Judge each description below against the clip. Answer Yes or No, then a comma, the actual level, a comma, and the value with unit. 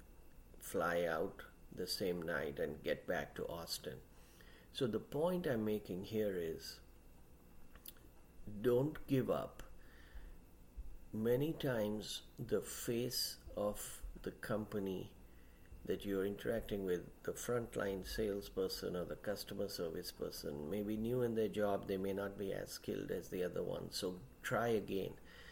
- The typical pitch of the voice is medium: No, low, 100 Hz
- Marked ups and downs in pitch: Yes, wide, 6.7 semitones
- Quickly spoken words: No, slow, 135 wpm